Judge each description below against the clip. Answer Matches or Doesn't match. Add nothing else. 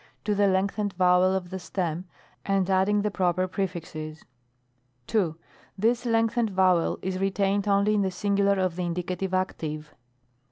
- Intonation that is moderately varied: Doesn't match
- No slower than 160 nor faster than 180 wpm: Doesn't match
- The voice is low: Doesn't match